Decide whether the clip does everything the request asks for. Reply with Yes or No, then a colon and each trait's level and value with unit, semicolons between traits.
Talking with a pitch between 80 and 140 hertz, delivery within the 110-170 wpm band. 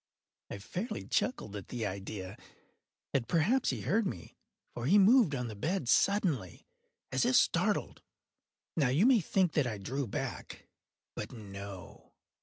Yes: low, 135 Hz; average, 145 wpm